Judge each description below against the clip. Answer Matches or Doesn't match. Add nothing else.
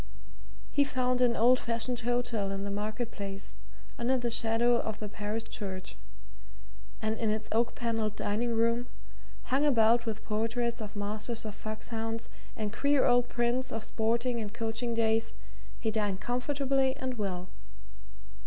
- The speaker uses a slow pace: Doesn't match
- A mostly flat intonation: Matches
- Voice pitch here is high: Matches